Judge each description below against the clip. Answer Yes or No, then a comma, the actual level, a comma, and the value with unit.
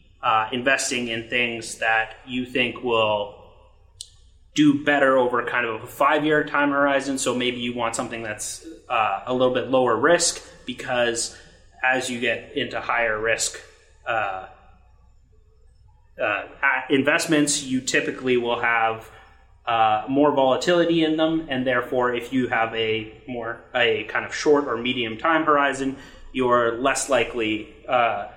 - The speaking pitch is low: Yes, low, 120 Hz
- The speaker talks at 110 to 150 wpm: Yes, average, 140 wpm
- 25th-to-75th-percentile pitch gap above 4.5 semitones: No, average, 3.3 semitones